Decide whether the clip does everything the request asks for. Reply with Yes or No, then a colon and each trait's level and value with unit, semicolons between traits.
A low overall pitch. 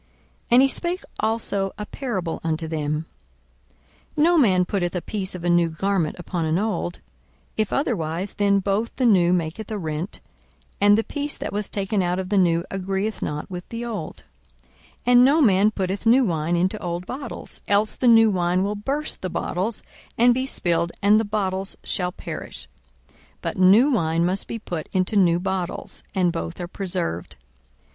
No: high, 190 Hz